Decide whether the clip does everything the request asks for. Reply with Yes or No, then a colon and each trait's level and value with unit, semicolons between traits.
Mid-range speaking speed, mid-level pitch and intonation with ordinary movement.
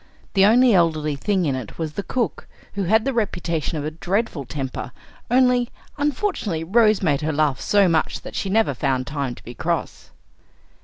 No: average, 185 wpm; medium, 175 Hz; wide, 6.8 semitones